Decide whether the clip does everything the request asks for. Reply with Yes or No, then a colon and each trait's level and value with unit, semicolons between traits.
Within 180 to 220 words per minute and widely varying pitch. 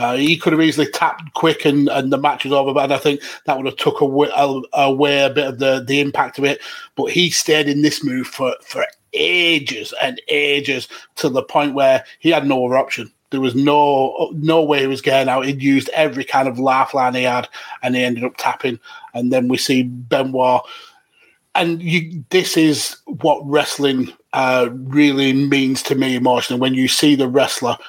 No: fast, 205 wpm; narrow, 2.5 semitones